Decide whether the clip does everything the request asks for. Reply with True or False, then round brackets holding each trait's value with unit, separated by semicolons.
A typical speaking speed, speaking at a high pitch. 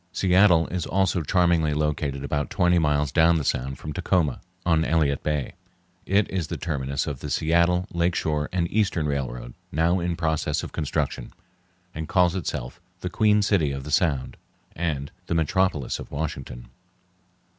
False (160 wpm; 80 Hz)